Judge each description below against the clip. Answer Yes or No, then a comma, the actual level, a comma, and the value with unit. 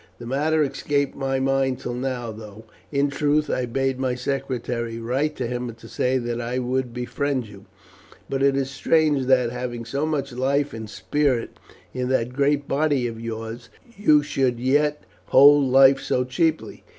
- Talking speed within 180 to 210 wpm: No, average, 170 wpm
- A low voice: Yes, low, 130 Hz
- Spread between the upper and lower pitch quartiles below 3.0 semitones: Yes, narrow, 2.6 semitones